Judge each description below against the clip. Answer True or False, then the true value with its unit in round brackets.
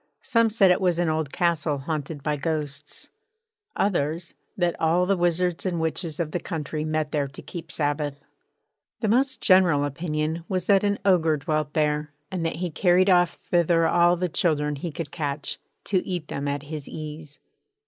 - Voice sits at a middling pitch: True (160 Hz)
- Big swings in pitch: False (3.0 semitones)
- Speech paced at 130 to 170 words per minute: False (180 wpm)